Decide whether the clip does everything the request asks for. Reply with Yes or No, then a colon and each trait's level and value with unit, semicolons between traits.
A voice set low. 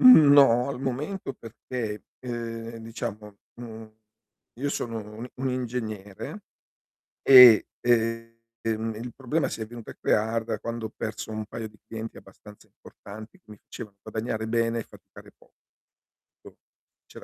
Yes: low, 115 Hz